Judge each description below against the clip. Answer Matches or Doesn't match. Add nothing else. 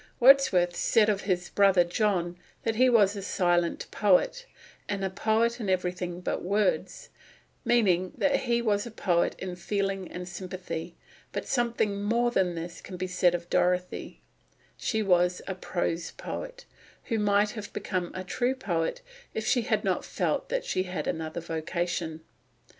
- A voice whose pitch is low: Doesn't match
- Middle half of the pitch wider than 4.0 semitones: Doesn't match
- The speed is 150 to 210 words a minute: Matches